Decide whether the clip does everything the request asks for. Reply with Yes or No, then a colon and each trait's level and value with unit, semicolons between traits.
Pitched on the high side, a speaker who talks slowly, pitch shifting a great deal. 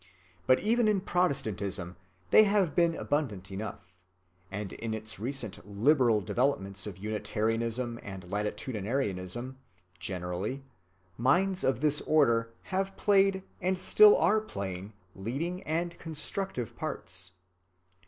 No: low, 120 Hz; slow, 115 wpm; wide, 9.0 semitones